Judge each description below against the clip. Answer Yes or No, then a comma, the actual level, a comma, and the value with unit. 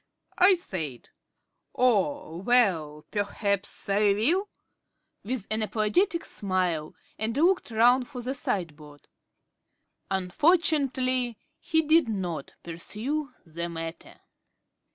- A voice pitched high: Yes, high, 215 Hz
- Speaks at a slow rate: Yes, slow, 95 wpm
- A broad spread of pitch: Yes, wide, 6.8 semitones